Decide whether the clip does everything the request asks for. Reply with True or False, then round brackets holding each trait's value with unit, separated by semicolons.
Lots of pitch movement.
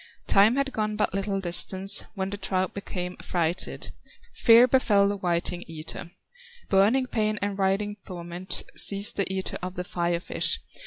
False (2.4 semitones)